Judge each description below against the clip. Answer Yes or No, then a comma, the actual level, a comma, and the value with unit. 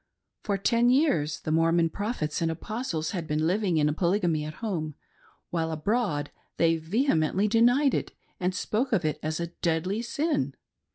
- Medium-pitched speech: Yes, medium, 170 Hz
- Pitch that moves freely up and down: Yes, wide, 5.7 semitones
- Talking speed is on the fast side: No, average, 160 wpm